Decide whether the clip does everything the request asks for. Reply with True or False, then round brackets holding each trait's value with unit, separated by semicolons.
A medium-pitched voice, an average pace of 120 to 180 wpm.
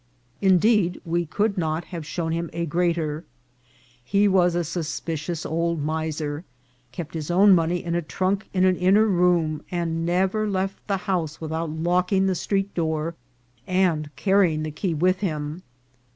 True (175 Hz; 160 wpm)